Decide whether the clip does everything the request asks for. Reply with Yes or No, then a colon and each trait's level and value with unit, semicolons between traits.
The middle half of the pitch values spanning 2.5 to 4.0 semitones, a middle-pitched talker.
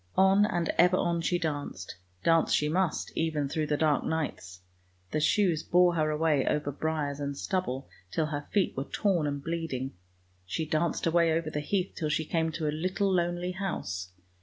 Yes: average, 3.0 semitones; medium, 160 Hz